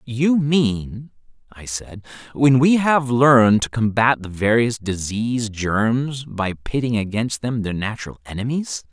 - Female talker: No, male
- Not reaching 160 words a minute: Yes, average, 140 wpm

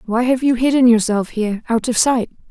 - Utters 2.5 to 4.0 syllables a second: No, 5.6 syllables/s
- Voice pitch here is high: Yes, high, 235 Hz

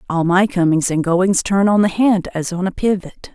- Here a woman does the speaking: Yes, female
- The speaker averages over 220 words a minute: Yes, fast, 235 wpm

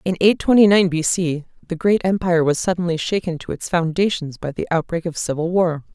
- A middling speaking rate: No, fast, 210 wpm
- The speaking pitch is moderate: Yes, medium, 175 Hz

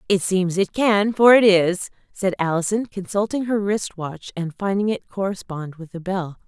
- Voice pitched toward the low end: No, high, 195 Hz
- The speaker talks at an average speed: Yes, average, 175 wpm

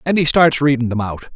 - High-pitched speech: No, medium, 140 Hz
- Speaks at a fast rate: Yes, fast, 265 wpm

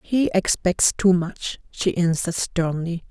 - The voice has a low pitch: No, medium, 180 Hz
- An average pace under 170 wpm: Yes, slow, 135 wpm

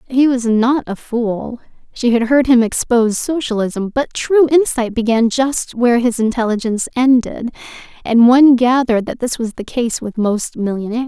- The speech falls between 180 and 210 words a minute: No, average, 155 wpm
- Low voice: No, high, 240 Hz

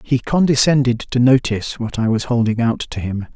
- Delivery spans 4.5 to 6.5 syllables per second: Yes, 5.3 syllables/s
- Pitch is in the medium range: No, low, 120 Hz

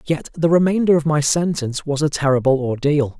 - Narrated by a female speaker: No, male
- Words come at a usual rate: Yes, average, 190 wpm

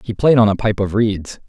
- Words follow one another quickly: Yes, fast, 285 wpm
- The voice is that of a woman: No, male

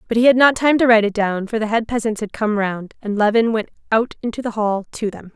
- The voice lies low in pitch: No, high, 220 Hz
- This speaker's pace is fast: Yes, fast, 280 wpm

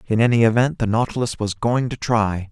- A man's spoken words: Yes, male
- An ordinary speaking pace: No, fast, 215 wpm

